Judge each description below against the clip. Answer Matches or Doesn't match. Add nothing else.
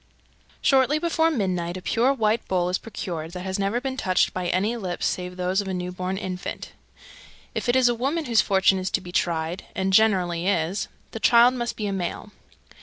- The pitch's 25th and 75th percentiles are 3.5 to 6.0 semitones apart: Matches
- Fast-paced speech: Matches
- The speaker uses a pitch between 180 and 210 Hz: Matches